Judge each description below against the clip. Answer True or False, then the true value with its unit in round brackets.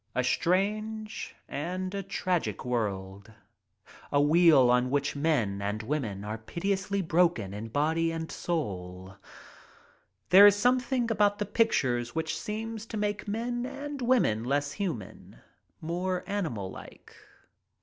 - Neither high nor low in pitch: True (165 Hz)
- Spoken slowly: True (130 wpm)